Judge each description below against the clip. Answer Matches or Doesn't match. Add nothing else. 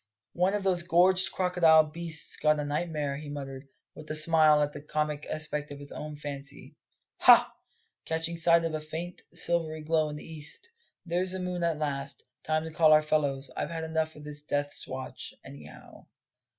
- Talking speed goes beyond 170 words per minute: Matches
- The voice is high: Doesn't match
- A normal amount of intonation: Doesn't match